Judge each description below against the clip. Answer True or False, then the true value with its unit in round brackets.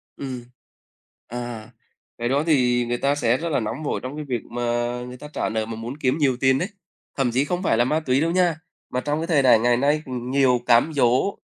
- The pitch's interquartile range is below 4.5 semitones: True (3.5 semitones)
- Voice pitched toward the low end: True (130 Hz)